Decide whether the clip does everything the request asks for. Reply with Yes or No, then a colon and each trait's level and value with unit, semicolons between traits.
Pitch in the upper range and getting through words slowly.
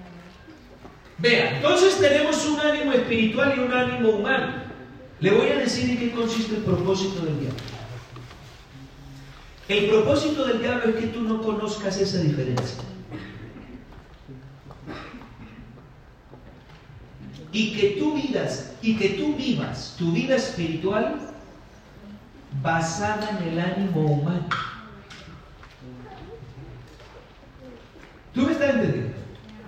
Yes: high, 195 Hz; slow, 105 wpm